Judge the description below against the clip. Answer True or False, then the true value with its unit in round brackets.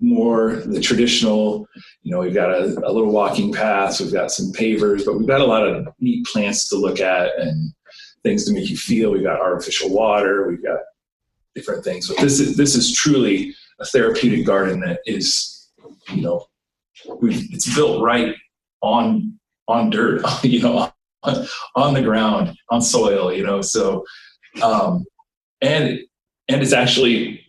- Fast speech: False (170 wpm)